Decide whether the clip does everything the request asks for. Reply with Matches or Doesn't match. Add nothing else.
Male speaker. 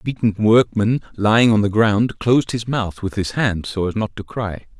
Matches